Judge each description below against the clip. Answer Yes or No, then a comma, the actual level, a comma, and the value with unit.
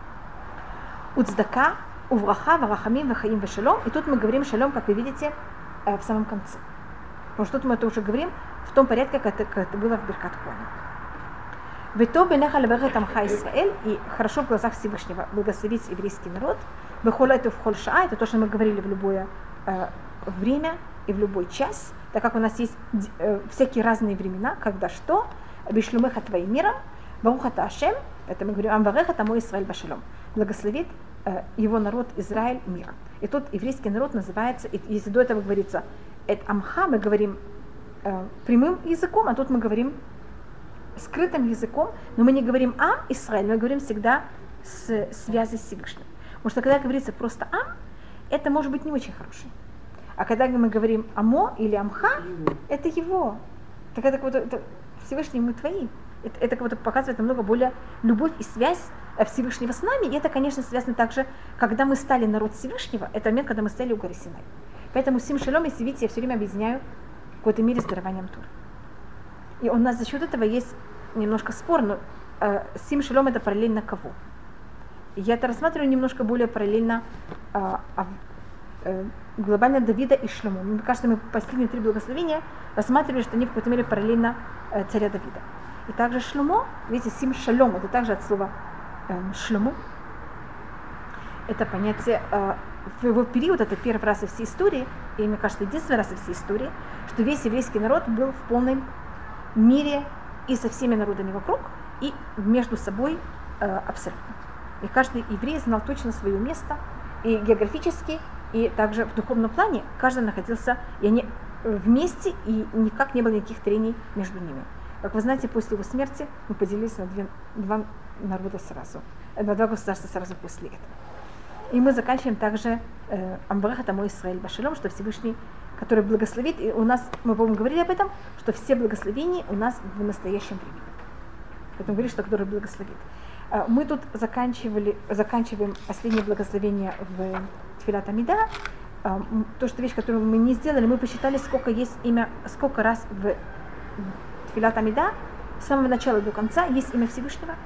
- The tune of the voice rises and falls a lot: No, average, 3.5 semitones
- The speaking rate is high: Yes, fast, 165 wpm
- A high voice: Yes, high, 230 Hz